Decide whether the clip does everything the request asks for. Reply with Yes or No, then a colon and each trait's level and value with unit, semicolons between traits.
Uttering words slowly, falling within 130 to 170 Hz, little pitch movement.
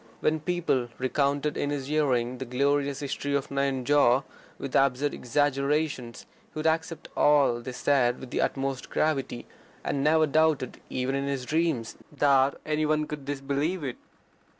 No: average, 150 wpm; medium, 140 Hz; narrow, 2.3 semitones